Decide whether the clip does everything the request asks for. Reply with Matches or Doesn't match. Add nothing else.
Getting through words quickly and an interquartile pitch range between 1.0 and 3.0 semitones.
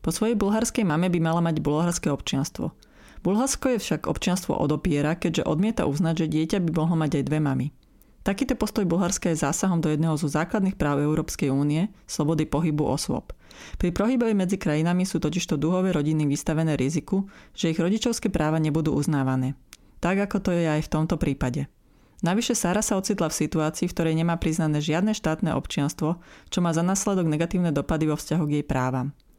Doesn't match